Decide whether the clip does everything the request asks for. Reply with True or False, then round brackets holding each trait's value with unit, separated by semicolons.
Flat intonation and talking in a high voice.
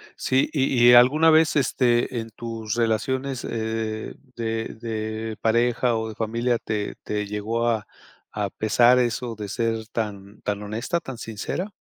False (2.0 semitones; 115 Hz)